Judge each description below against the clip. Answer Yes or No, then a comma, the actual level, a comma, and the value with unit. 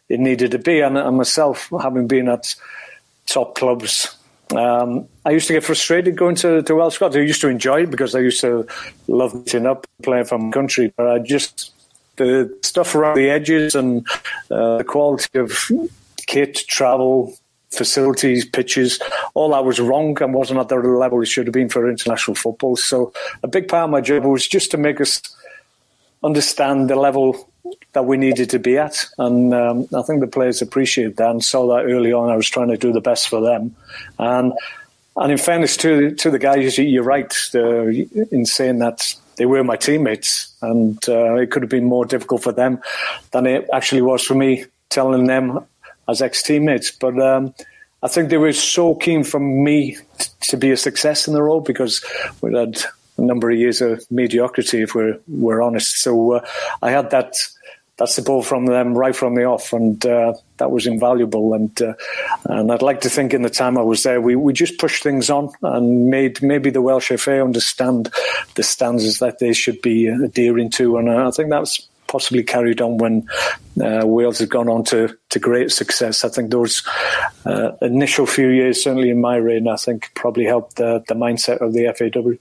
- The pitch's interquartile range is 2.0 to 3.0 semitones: Yes, narrow, 2.6 semitones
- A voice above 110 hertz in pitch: Yes, low, 125 Hz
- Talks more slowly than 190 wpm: No, fast, 205 wpm